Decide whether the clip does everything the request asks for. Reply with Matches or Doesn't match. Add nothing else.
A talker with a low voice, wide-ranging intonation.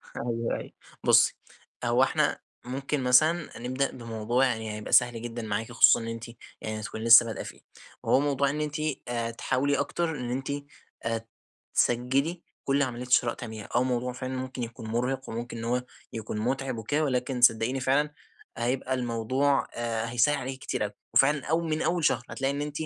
Doesn't match